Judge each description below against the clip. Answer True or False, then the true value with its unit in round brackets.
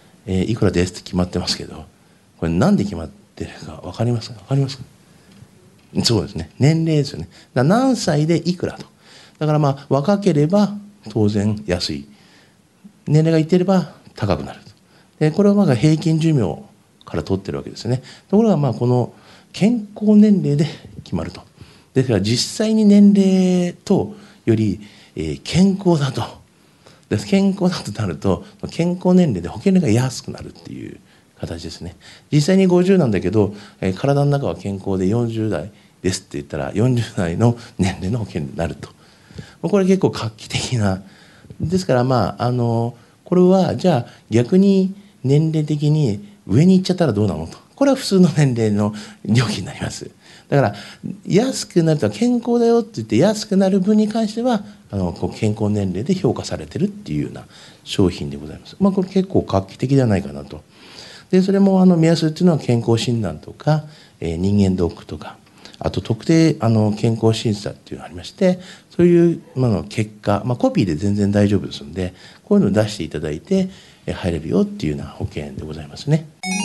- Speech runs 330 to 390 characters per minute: True (340 characters per minute)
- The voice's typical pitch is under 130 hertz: False (135 Hz)